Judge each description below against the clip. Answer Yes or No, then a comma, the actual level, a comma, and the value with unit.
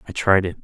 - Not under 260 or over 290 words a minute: Yes, fast, 285 wpm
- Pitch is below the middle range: Yes, very low, 95 Hz